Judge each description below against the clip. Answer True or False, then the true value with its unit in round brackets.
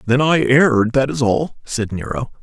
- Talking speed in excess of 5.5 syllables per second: False (4.7 syllables/s)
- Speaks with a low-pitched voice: True (125 Hz)